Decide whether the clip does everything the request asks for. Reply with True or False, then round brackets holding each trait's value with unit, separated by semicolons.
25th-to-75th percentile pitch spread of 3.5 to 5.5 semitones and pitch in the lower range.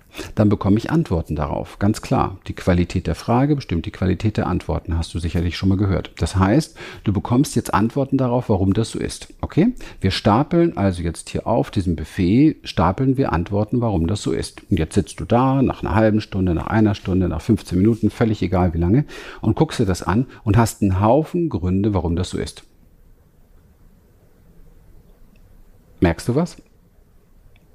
True (4.3 semitones; 100 Hz)